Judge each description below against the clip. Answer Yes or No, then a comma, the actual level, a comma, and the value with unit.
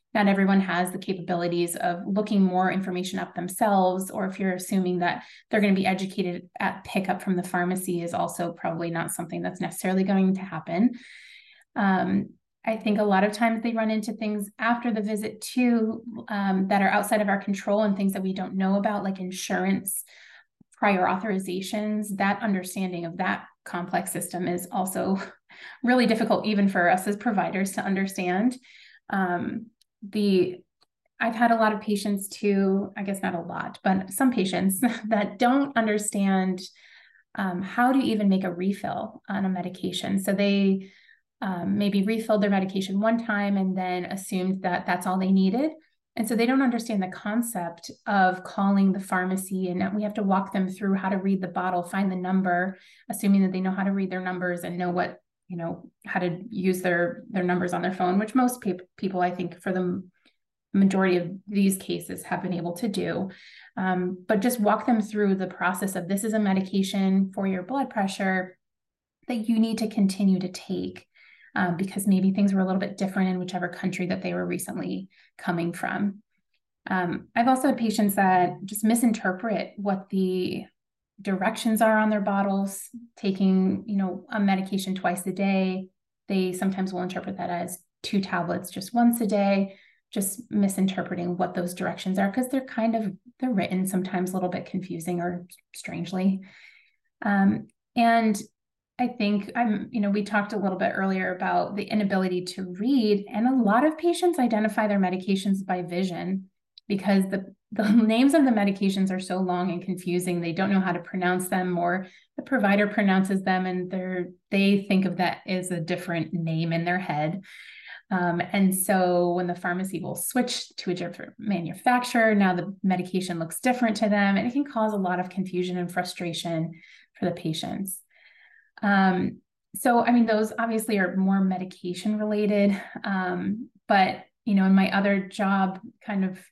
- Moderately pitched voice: No, high, 195 Hz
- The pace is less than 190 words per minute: Yes, average, 180 wpm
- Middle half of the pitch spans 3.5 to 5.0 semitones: No, narrow, 2.6 semitones